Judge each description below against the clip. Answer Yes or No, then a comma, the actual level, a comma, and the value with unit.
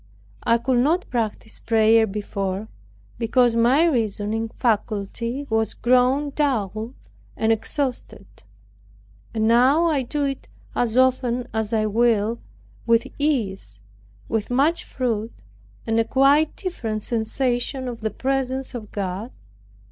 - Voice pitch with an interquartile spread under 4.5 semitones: Yes, average, 3.2 semitones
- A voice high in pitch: Yes, high, 235 Hz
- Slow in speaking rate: Yes, slow, 120 wpm